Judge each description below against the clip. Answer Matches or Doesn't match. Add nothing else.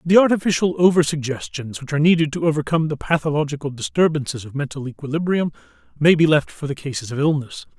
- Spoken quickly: Doesn't match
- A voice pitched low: Doesn't match